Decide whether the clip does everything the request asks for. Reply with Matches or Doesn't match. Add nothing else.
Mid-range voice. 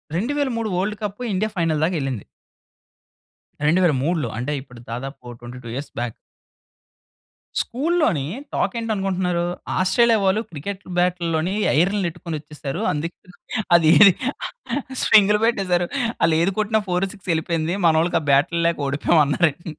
Matches